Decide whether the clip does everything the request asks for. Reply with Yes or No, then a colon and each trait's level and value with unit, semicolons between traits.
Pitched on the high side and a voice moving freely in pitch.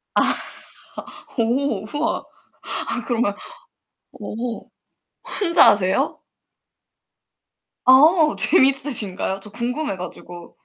Yes: high, 240 Hz; wide, 5.9 semitones